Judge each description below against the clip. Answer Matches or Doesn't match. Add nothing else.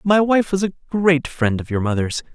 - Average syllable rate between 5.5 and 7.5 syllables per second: Doesn't match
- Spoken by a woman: Doesn't match